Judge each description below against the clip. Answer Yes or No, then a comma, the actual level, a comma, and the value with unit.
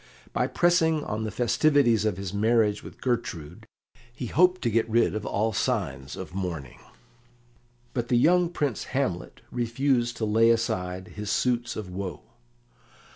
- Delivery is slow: No, average, 150 wpm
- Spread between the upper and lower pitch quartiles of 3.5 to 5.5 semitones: Yes, average, 3.9 semitones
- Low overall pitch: Yes, low, 115 Hz